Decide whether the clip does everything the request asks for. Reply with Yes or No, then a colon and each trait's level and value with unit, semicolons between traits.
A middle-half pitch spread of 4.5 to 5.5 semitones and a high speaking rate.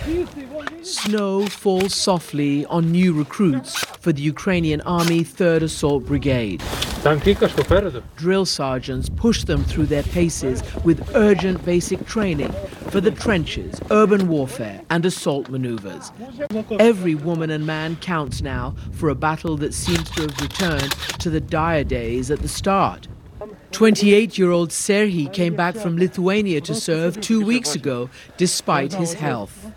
No: average, 5.1 semitones; slow, 135 wpm